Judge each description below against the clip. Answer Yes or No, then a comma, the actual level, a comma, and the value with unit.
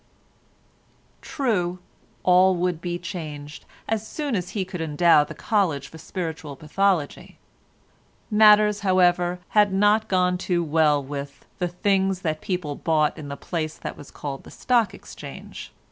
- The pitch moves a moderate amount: Yes, average, 4.1 semitones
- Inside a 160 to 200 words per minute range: No, average, 145 wpm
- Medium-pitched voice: Yes, medium, 180 Hz